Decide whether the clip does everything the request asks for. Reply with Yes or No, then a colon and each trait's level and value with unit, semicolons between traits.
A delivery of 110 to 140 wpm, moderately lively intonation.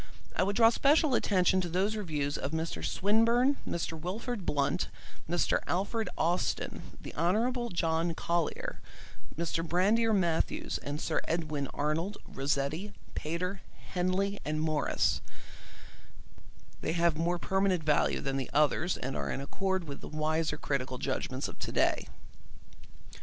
Yes: slow, 135 wpm; average, 4.3 semitones